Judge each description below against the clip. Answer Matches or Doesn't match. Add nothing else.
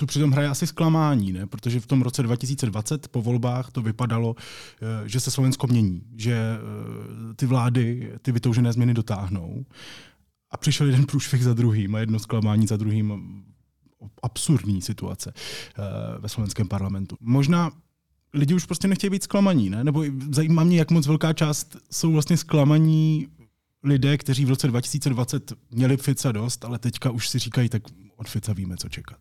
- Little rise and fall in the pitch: Doesn't match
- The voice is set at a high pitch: Doesn't match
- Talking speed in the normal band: Matches